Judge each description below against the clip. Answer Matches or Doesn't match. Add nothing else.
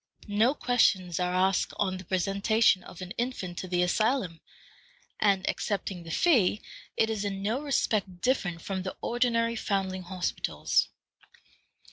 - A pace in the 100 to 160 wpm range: Matches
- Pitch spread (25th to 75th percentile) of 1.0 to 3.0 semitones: Doesn't match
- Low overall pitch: Doesn't match